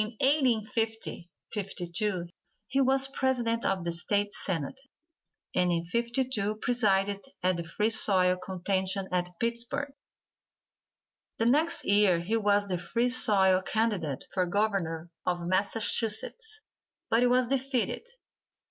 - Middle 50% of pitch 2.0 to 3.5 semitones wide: No, average, 4.5 semitones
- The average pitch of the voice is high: Yes, high, 205 Hz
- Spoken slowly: Yes, slow, 120 wpm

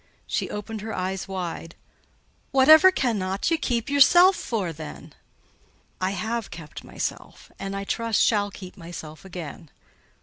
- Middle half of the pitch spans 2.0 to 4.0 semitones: No, average, 4.5 semitones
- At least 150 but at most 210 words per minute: No, slow, 135 wpm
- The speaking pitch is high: Yes, high, 200 Hz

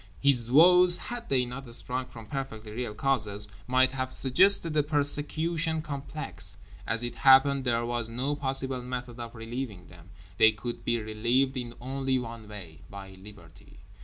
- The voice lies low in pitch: Yes, low, 125 Hz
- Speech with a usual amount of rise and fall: Yes, average, 3.9 semitones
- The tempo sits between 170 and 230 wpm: No, average, 155 wpm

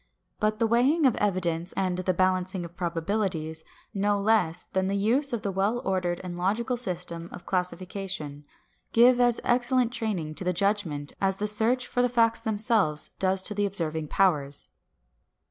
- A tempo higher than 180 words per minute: No, average, 165 wpm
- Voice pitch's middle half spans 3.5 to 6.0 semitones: Yes, average, 4.1 semitones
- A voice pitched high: Yes, high, 195 Hz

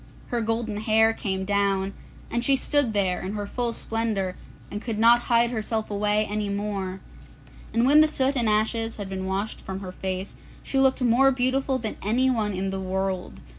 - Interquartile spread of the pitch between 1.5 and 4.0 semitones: Yes, average, 3.5 semitones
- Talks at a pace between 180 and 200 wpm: Yes, average, 185 wpm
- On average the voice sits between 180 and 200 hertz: No, high, 215 Hz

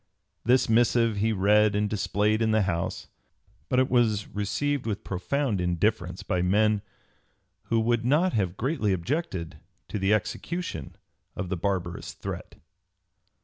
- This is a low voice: Yes, low, 105 Hz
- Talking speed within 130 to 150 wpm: Yes, average, 140 wpm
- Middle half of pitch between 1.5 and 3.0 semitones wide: No, average, 3.8 semitones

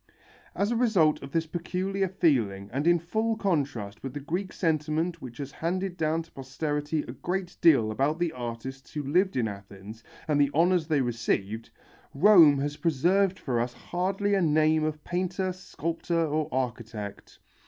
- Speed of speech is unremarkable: Yes, average, 165 wpm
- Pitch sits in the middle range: Yes, medium, 155 Hz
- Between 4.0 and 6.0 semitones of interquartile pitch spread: Yes, average, 5.1 semitones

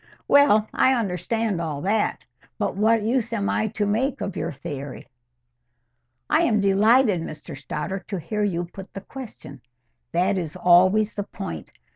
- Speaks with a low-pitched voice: No, high, 200 Hz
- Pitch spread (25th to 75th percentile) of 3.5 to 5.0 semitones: Yes, average, 4.1 semitones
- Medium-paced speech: Yes, average, 155 wpm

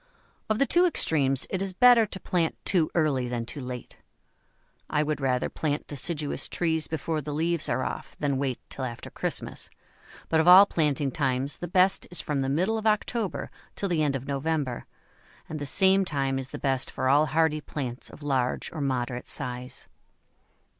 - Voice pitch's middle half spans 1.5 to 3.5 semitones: No, average, 4.5 semitones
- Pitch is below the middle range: No, medium, 150 Hz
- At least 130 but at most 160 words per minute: No, average, 185 wpm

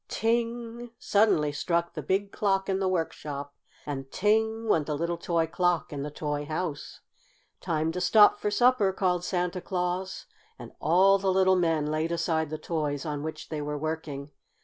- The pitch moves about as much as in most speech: Yes, average, 4.0 semitones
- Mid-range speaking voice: Yes, medium, 170 Hz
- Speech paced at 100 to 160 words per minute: No, average, 170 wpm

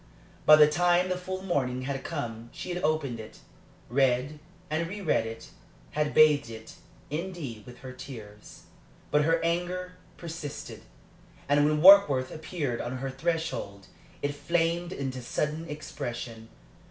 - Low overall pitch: No, medium, 150 Hz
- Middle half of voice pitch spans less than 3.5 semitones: No, average, 4.7 semitones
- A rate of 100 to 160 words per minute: Yes, average, 140 wpm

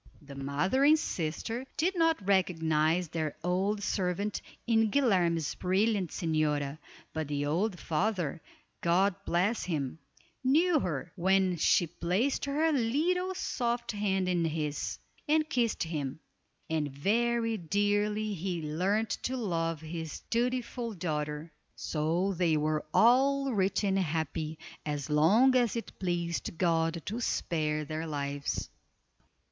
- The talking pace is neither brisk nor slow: No, slow, 125 wpm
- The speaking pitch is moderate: Yes, medium, 180 Hz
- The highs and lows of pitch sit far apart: Yes, wide, 6.3 semitones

